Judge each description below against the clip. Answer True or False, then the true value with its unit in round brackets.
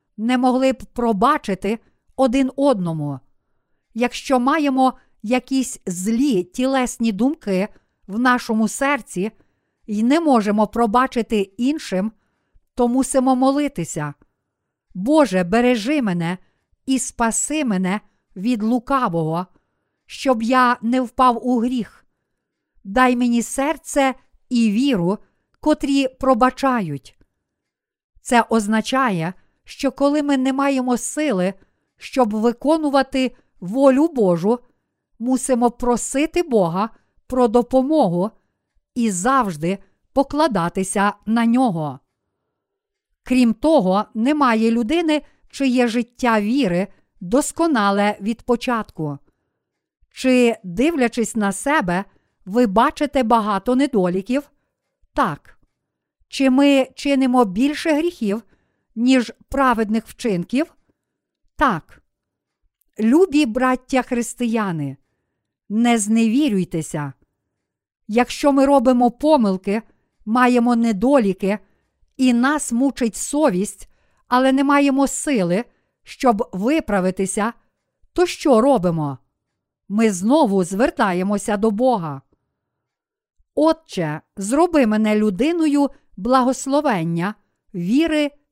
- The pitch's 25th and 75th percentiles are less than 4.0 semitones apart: False (4.8 semitones)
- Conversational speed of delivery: False (85 wpm)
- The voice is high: True (245 Hz)